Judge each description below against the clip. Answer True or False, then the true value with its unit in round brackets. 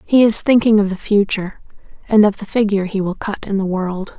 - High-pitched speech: True (205 Hz)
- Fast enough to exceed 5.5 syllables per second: True (5.8 syllables/s)